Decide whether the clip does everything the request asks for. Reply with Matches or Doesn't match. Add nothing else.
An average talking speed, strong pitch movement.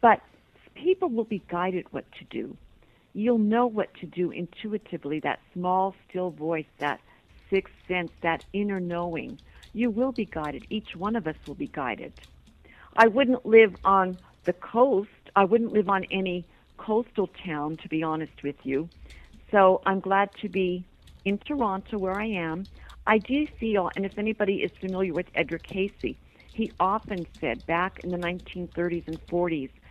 Doesn't match